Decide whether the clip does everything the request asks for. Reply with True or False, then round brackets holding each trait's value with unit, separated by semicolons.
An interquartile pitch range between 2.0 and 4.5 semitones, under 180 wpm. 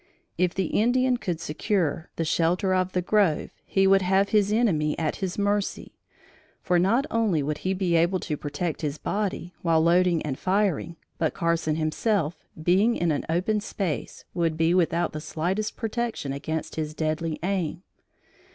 True (3.8 semitones; 165 wpm)